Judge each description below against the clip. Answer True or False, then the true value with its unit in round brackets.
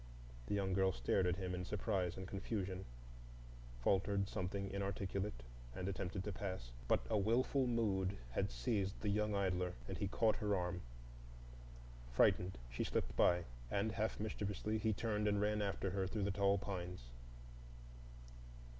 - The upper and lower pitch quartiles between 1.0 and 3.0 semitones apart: True (2.4 semitones)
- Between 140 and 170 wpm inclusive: True (155 wpm)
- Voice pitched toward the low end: True (95 Hz)